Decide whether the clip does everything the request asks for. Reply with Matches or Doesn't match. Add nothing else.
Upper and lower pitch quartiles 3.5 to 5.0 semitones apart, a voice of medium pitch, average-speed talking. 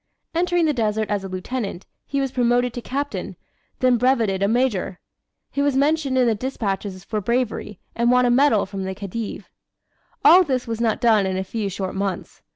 Doesn't match